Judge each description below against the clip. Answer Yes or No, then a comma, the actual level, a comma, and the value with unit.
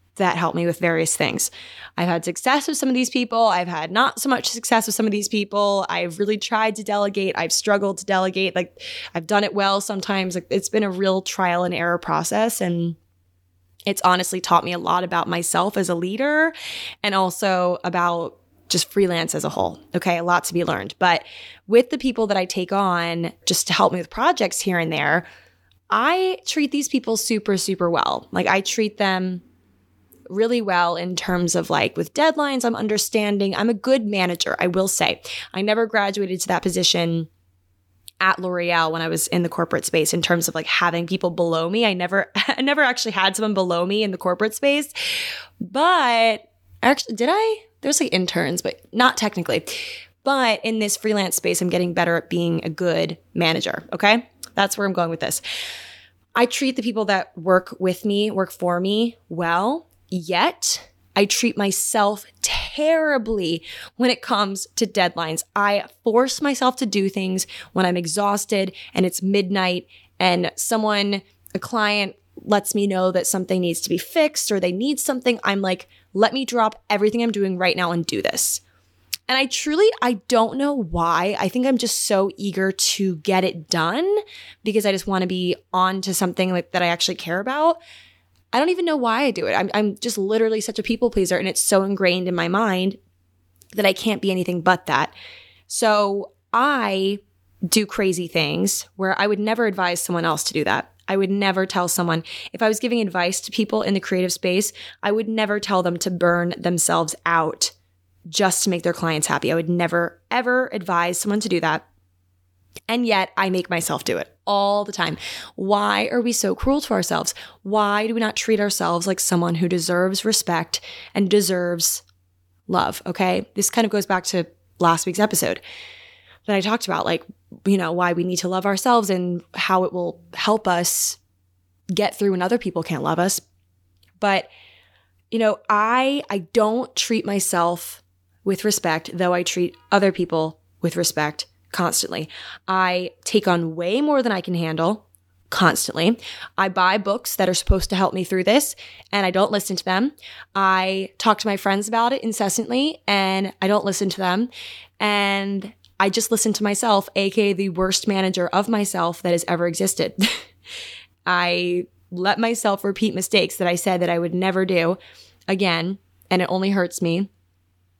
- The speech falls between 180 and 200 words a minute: Yes, average, 190 wpm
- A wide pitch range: No, average, 3.8 semitones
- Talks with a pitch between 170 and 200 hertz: Yes, high, 190 Hz